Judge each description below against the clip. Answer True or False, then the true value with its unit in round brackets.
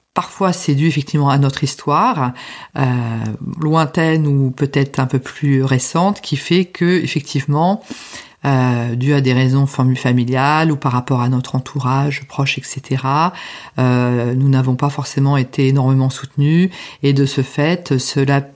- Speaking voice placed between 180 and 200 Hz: False (140 Hz)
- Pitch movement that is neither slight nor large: True (3.0 semitones)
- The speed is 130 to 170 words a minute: True (150 wpm)